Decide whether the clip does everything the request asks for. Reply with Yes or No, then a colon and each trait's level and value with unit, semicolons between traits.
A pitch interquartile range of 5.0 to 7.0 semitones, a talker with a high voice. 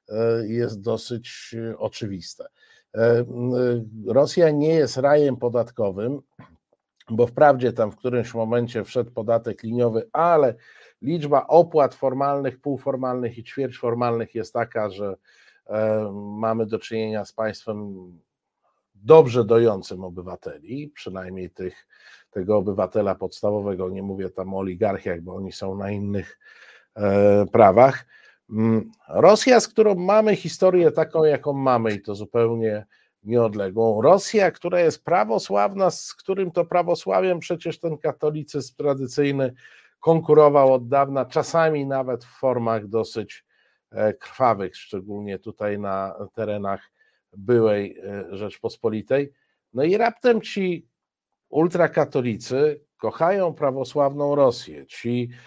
No: wide, 5.6 semitones; low, 120 Hz